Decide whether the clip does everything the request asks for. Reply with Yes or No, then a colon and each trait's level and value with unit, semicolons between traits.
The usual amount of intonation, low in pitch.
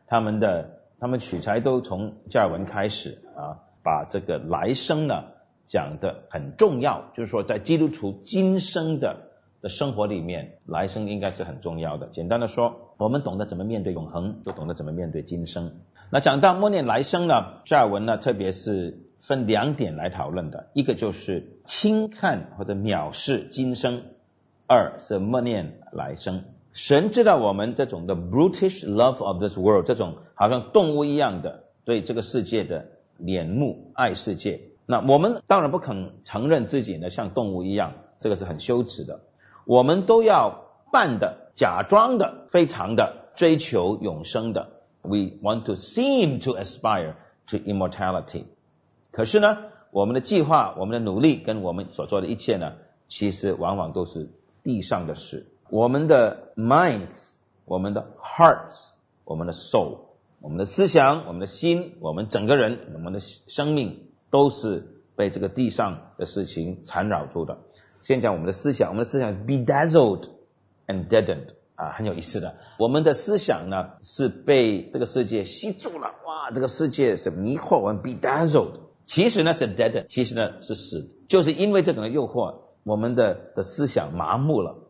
No: wide, 7.4 semitones; low, 115 Hz